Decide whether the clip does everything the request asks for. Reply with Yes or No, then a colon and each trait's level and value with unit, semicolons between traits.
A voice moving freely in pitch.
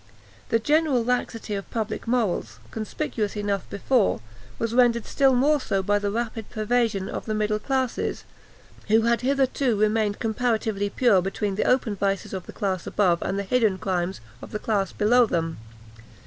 No: average, 3.3 semitones